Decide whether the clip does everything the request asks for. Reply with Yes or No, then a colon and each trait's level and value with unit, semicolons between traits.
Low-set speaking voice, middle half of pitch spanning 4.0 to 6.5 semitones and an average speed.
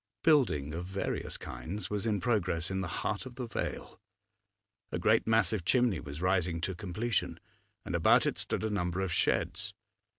Yes: very low, 95 Hz; average, 4.3 semitones; average, 170 wpm